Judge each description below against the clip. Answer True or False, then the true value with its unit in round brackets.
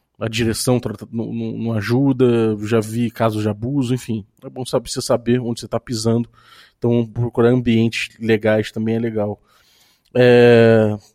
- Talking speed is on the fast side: False (140 wpm)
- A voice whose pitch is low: True (115 Hz)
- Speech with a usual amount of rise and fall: False (1.4 semitones)